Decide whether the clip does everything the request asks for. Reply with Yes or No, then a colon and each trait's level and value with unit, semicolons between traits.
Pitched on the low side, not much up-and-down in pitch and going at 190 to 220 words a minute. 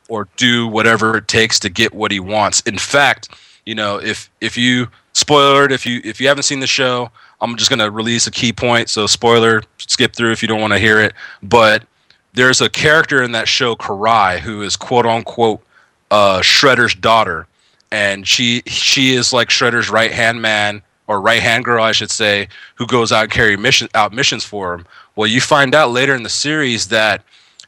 Yes: low, 115 Hz; narrow, 2.3 semitones; fast, 205 wpm